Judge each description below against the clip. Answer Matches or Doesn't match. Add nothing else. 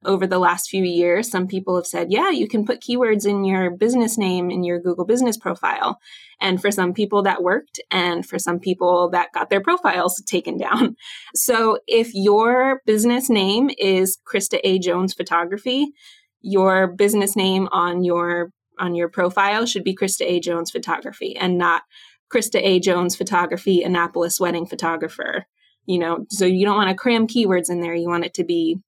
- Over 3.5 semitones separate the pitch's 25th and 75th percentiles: Doesn't match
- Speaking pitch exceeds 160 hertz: Matches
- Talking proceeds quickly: Doesn't match